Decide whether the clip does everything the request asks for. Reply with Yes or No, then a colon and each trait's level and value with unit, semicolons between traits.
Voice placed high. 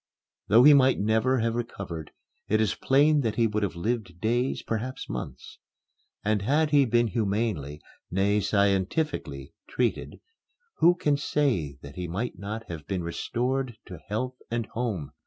No: low, 110 Hz